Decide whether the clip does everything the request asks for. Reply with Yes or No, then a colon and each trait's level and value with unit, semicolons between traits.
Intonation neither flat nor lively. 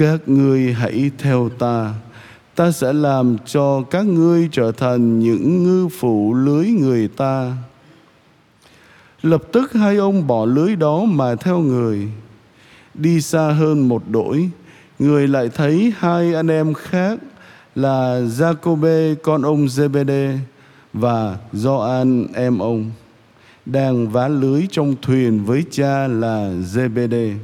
Yes: average, 5.0 semitones